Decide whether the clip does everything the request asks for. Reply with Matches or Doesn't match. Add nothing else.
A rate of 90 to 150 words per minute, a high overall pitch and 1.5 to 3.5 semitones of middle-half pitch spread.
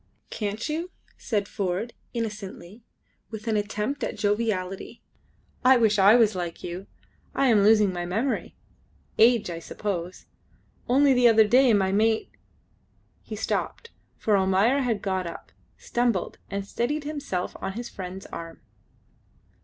Doesn't match